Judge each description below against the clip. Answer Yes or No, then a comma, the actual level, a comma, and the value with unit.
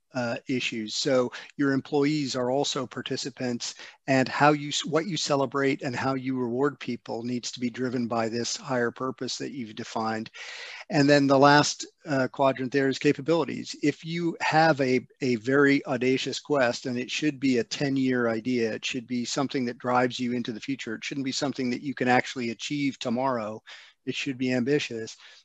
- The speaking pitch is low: Yes, low, 130 Hz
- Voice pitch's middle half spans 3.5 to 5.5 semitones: No, narrow, 2.5 semitones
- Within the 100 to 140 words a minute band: No, average, 185 wpm